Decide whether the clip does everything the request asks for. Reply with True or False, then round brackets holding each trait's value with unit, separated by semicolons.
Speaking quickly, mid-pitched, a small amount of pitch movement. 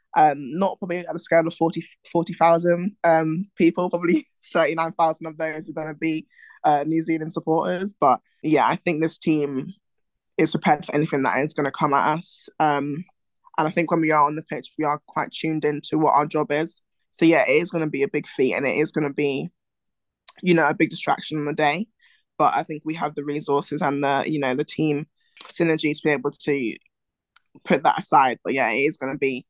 True (225 wpm; 155 Hz; 2.2 semitones)